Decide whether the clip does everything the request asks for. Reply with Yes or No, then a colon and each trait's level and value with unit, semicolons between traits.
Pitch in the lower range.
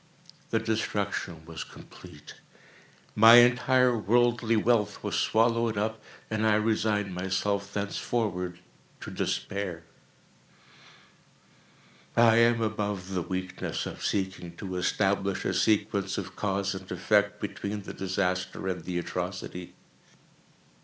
Yes: low, 100 Hz